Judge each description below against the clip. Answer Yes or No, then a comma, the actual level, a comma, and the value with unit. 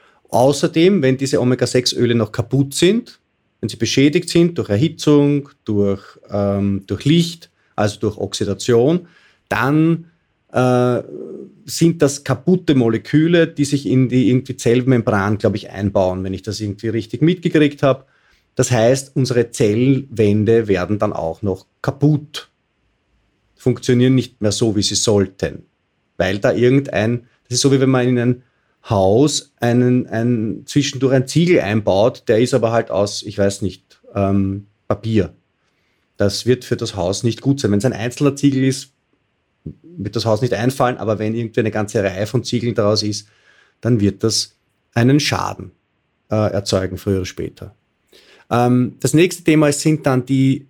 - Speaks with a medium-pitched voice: No, low, 120 Hz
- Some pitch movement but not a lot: Yes, average, 4.7 semitones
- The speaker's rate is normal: Yes, average, 155 wpm